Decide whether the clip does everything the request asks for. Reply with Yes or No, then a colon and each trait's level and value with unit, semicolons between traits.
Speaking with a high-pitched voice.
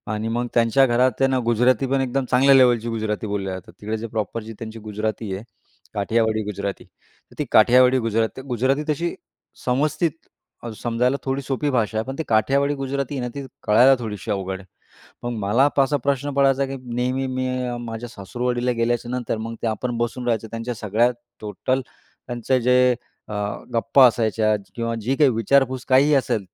No: low, 120 Hz